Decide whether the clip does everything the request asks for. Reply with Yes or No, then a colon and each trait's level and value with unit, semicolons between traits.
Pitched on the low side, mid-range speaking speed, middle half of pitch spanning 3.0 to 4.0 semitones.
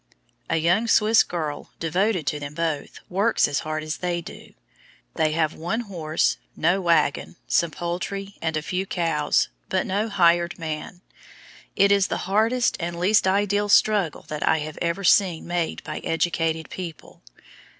No: medium, 175 Hz; average, 160 wpm; average, 3.6 semitones